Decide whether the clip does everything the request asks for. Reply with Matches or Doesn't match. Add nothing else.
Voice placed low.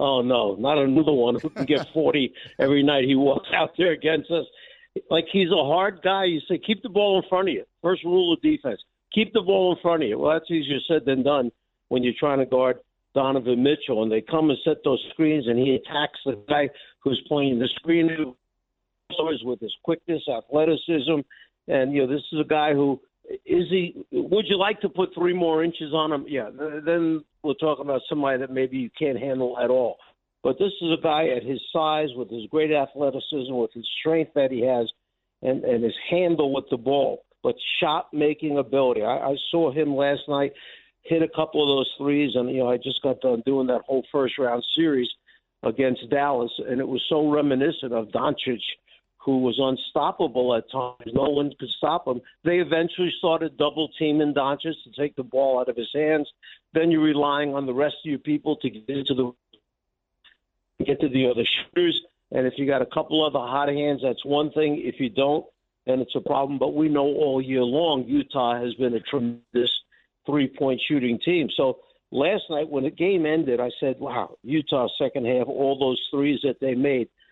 Doesn't match